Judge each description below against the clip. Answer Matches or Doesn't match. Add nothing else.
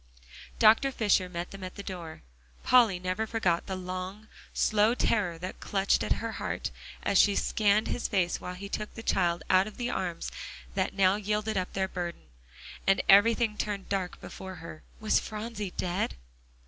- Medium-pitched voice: Doesn't match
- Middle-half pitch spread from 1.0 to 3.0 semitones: Matches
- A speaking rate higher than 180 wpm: Doesn't match